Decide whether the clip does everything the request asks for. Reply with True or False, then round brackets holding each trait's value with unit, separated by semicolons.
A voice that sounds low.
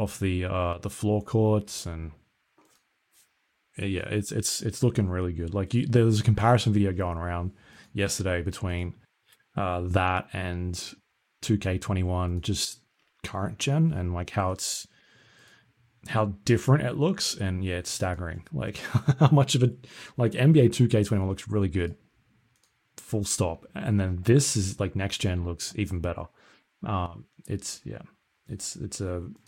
True (100 Hz)